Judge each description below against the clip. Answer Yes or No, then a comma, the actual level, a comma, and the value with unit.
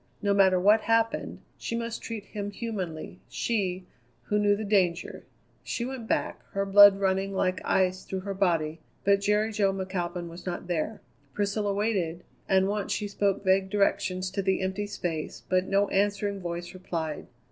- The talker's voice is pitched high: Yes, high, 195 Hz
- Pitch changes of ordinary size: No, narrow, 2.0 semitones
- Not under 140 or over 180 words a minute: Yes, average, 170 wpm